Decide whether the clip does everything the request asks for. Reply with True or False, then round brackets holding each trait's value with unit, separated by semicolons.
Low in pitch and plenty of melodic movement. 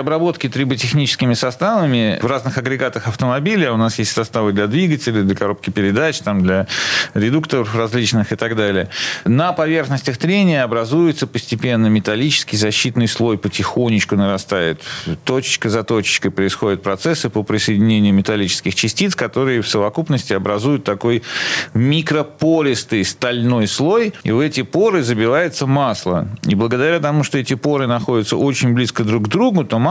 False (120 Hz; 4.6 semitones)